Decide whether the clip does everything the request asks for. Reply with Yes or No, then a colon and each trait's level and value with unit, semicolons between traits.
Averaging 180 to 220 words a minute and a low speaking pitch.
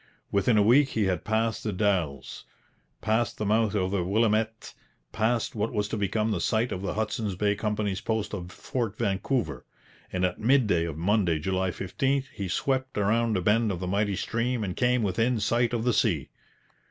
Yes: average, 190 wpm; low, 105 Hz